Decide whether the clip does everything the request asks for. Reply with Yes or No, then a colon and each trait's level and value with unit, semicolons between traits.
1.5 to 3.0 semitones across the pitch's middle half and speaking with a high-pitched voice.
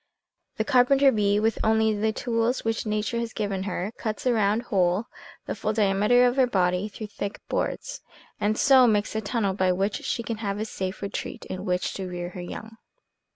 Yes: average, 2.7 semitones; high, 215 Hz